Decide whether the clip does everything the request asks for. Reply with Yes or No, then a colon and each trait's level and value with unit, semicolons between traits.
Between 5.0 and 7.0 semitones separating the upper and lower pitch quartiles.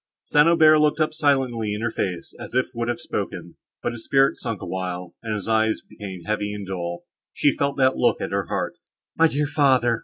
Yes: wide, 5.4 semitones